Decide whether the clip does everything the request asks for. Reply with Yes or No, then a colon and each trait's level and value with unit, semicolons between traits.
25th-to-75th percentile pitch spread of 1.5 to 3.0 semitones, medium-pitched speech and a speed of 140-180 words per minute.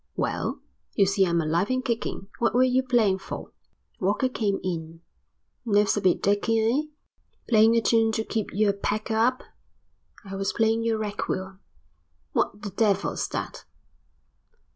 No: average, 2.7 semitones; high, 210 Hz; average, 150 wpm